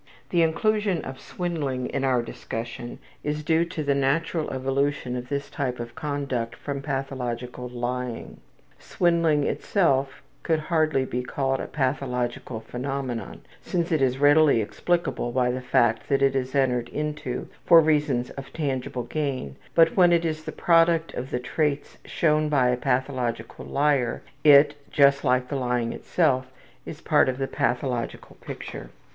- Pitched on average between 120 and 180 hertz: Yes, low, 135 Hz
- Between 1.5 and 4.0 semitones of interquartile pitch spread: Yes, average, 3.5 semitones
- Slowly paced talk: No, average, 155 wpm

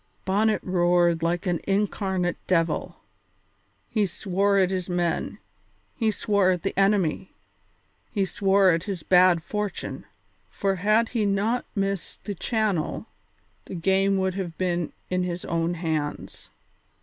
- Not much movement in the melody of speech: Yes, narrow, 2.3 semitones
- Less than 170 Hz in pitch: No, high, 190 Hz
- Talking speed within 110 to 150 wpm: Yes, slow, 135 wpm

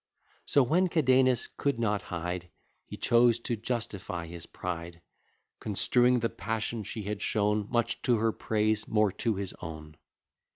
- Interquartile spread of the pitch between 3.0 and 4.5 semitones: Yes, average, 4.1 semitones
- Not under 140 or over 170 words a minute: Yes, average, 150 wpm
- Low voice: Yes, low, 110 Hz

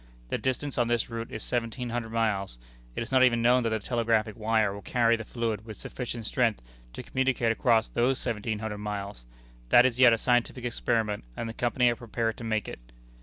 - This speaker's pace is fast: Yes, fast, 210 wpm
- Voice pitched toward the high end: No, low, 115 Hz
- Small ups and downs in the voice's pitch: Yes, narrow, 1.9 semitones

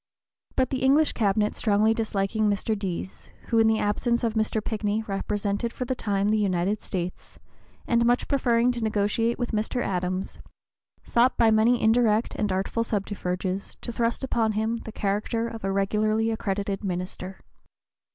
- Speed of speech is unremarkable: Yes, average, 160 wpm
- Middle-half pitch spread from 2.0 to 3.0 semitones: Yes, average, 2.7 semitones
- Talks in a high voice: Yes, high, 215 Hz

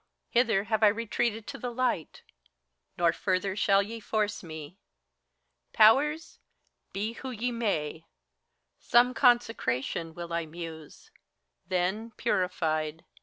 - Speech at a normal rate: No, slow, 115 wpm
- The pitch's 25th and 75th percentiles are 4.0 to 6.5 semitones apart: Yes, wide, 5.6 semitones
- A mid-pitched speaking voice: No, high, 205 Hz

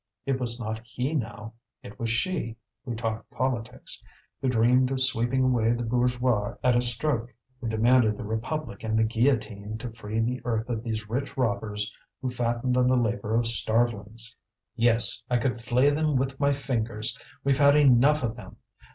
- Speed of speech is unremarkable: Yes, average, 175 wpm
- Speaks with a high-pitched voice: No, low, 120 Hz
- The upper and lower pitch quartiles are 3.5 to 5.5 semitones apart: No, narrow, 2.4 semitones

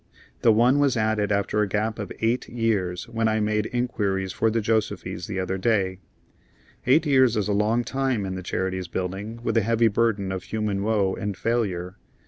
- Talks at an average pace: Yes, average, 190 wpm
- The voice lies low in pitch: Yes, low, 105 Hz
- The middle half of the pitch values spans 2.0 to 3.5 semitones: Yes, average, 3.1 semitones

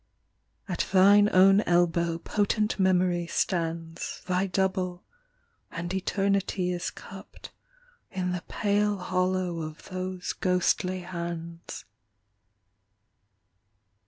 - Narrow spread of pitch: Yes, narrow, 1.7 semitones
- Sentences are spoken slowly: Yes, slow, 90 wpm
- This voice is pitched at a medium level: Yes, medium, 180 Hz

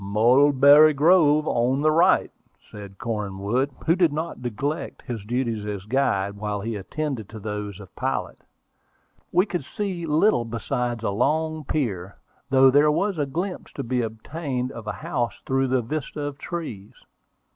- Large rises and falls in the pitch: Yes, wide, 6.2 semitones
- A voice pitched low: Yes, low, 130 Hz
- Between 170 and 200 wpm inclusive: No, average, 155 wpm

